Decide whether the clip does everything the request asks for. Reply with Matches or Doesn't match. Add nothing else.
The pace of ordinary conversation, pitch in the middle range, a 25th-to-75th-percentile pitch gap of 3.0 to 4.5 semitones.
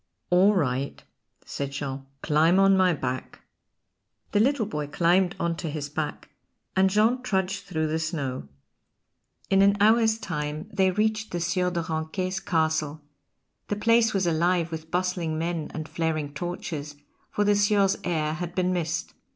Matches